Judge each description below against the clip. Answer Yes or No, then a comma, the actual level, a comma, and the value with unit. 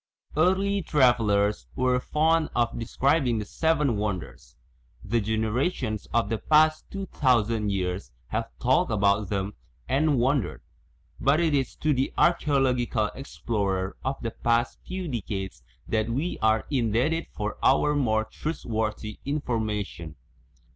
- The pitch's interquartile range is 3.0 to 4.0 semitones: No, wide, 5.5 semitones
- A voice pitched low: Yes, low, 120 Hz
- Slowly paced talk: Yes, slow, 130 wpm